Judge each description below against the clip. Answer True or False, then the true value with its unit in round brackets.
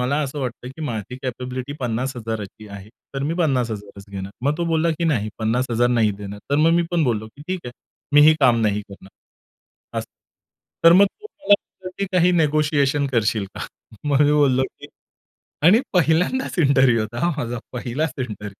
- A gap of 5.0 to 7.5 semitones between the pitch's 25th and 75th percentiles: True (5.3 semitones)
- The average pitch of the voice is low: True (130 Hz)